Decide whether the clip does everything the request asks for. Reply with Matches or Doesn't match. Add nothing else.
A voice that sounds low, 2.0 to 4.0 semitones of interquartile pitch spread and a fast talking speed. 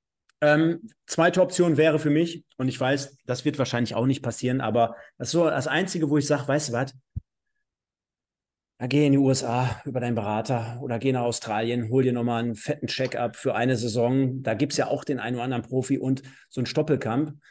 Matches